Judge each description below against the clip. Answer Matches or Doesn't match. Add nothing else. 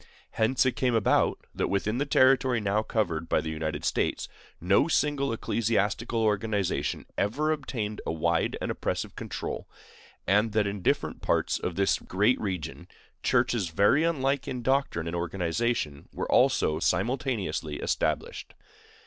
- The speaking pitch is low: Matches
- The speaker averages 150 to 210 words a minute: Doesn't match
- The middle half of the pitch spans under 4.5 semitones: Doesn't match